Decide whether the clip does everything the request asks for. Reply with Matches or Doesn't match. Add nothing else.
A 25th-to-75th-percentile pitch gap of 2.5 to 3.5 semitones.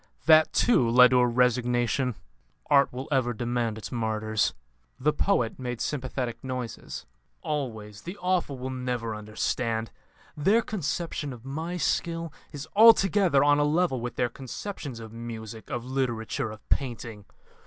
Doesn't match